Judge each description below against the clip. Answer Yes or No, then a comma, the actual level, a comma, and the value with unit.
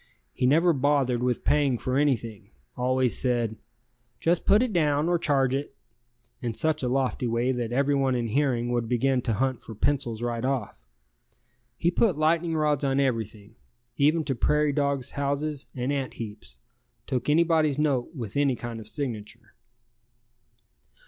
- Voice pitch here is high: No, low, 135 Hz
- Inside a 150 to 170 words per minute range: Yes, average, 155 wpm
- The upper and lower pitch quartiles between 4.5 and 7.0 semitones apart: No, average, 3.5 semitones